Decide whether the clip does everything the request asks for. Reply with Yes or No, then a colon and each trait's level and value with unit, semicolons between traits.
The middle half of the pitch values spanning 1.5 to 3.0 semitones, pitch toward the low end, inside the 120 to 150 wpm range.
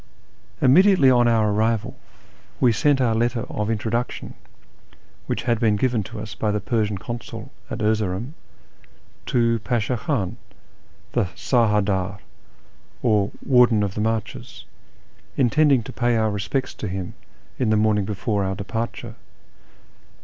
Yes: average, 2.7 semitones; low, 110 Hz; average, 140 wpm